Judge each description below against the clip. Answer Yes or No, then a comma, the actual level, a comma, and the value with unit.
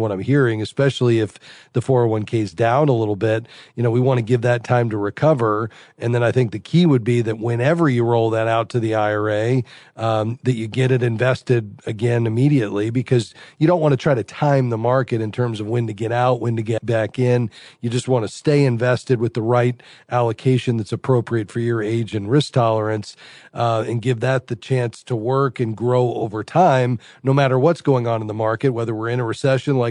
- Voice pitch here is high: No, low, 120 Hz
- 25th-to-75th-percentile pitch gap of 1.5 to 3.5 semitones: Yes, narrow, 2.4 semitones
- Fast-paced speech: Yes, fast, 225 wpm